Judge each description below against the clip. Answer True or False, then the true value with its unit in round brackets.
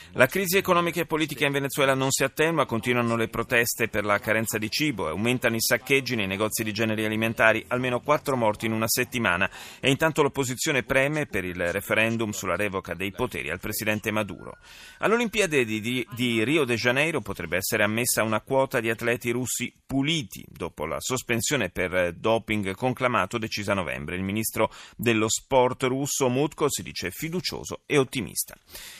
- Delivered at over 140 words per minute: True (170 wpm)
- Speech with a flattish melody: False (3.8 semitones)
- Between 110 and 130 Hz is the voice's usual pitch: True (115 Hz)